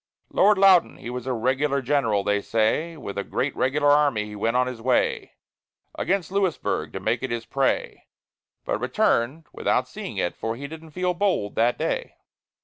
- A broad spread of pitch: Yes, wide, 5.9 semitones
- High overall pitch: No, low, 130 Hz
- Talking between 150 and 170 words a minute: No, average, 180 wpm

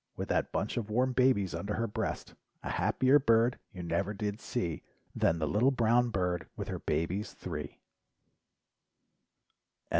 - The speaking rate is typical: Yes, average, 150 wpm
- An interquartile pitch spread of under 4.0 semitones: No, average, 4.6 semitones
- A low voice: Yes, low, 105 Hz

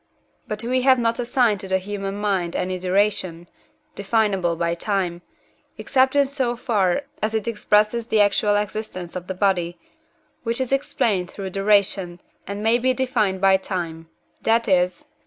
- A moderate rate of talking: Yes, average, 160 wpm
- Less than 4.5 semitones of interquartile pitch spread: Yes, average, 3.8 semitones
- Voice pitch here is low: No, high, 205 Hz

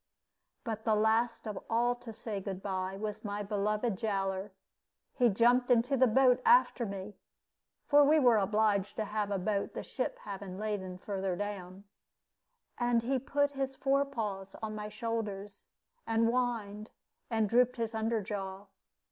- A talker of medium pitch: No, high, 215 Hz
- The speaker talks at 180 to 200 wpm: No, average, 155 wpm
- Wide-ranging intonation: No, average, 3.3 semitones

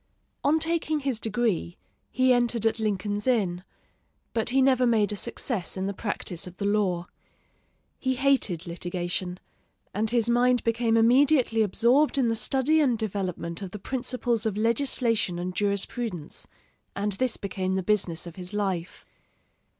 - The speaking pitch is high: Yes, high, 220 Hz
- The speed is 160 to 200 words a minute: No, average, 150 wpm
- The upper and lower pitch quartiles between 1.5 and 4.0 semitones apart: No, average, 4.5 semitones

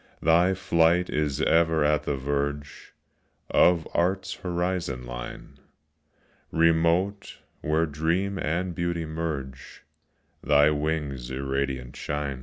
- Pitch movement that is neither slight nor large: Yes, average, 3.3 semitones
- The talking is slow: Yes, slow, 100 wpm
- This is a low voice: Yes, very low, 80 Hz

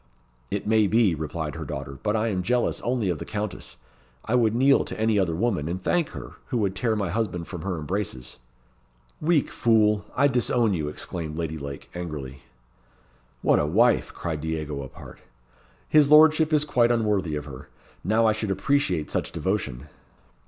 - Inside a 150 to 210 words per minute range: Yes, average, 175 wpm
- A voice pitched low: Yes, low, 100 Hz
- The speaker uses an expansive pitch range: Yes, wide, 6.7 semitones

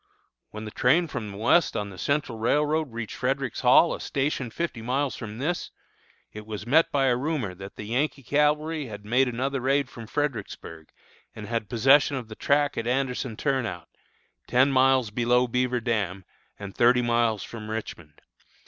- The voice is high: No, low, 125 Hz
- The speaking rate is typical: Yes, average, 175 wpm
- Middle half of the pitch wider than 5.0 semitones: No, average, 4.0 semitones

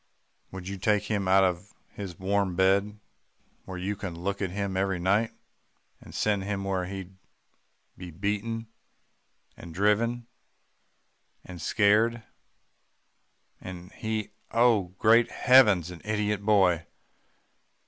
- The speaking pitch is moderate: No, low, 100 Hz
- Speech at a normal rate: No, slow, 120 wpm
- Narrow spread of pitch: Yes, narrow, 2.2 semitones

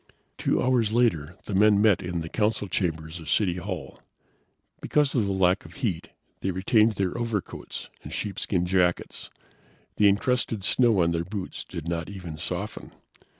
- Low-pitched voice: Yes, very low, 95 Hz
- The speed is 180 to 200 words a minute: No, average, 160 wpm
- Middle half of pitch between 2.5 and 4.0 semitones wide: Yes, average, 3.7 semitones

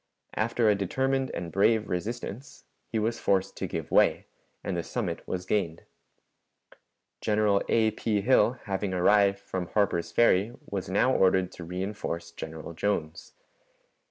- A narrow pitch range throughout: No, average, 3.3 semitones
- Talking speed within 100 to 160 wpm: Yes, average, 140 wpm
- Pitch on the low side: Yes, low, 100 Hz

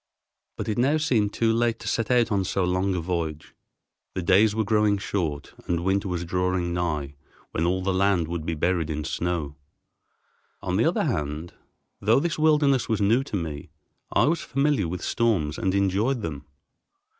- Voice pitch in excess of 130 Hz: No, very low, 95 Hz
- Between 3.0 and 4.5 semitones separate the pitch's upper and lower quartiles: No, average, 4.9 semitones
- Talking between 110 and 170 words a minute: No, average, 180 wpm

